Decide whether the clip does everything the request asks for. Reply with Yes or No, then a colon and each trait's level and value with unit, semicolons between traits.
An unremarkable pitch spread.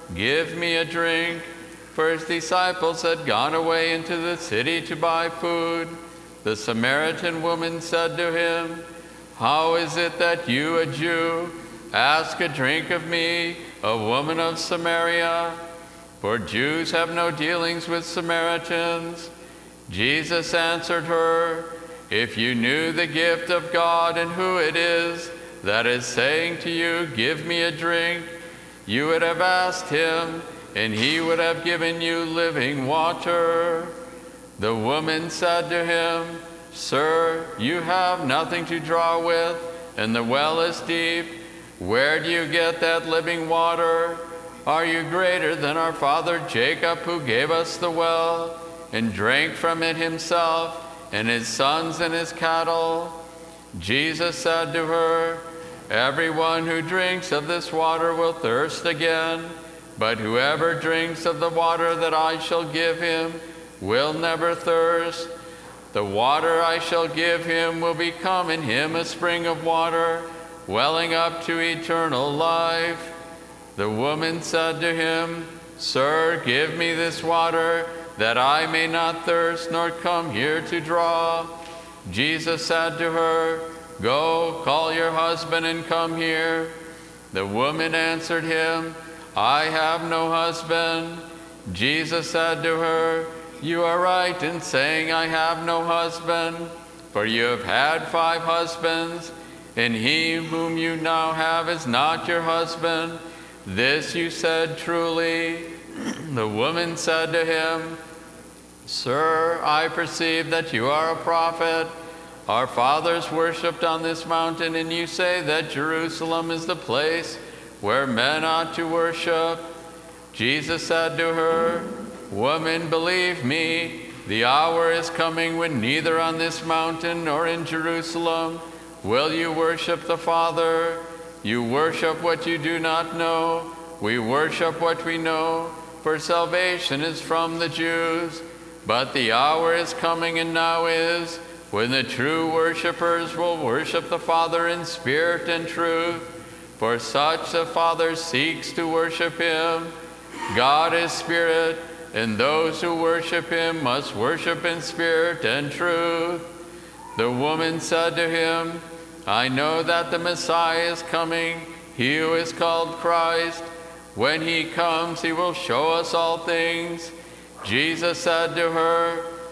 No: narrow, 0.5 semitones